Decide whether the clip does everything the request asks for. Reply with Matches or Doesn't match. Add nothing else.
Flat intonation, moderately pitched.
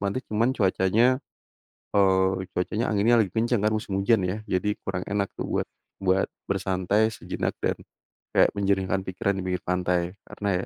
Doesn't match